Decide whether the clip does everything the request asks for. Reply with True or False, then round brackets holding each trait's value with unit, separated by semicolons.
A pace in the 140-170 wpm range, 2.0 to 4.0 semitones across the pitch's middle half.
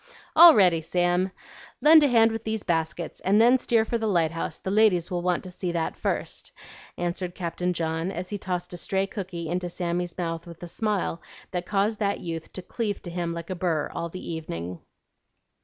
False (195 wpm; 3.2 semitones)